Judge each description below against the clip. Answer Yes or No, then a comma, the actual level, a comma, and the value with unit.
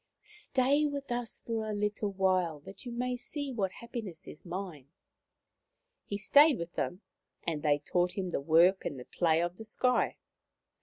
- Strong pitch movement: Yes, wide, 6.1 semitones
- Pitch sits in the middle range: No, high, 200 Hz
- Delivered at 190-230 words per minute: No, average, 170 wpm